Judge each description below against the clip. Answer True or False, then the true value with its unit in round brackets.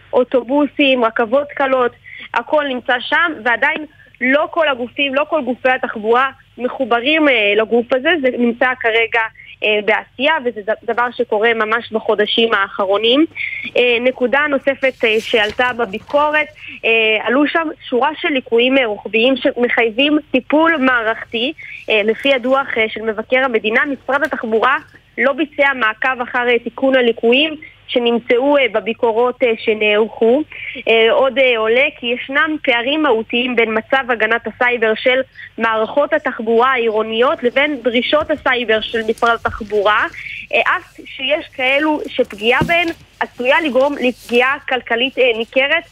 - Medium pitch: False (250 Hz)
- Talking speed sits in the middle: True (130 wpm)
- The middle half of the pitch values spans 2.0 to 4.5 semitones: True (3.3 semitones)